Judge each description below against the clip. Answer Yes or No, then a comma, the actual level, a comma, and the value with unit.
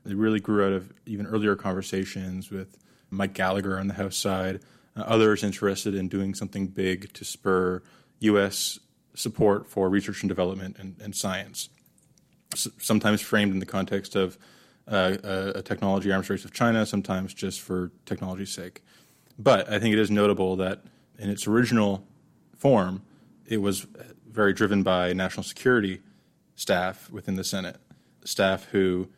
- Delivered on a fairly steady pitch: Yes, narrow, 1.9 semitones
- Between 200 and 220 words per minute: No, average, 155 wpm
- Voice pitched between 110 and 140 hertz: No, low, 100 Hz